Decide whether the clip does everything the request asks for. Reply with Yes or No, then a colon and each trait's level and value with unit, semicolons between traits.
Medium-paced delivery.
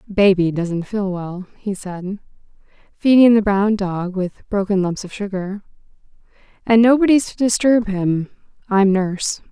No: slow, 130 wpm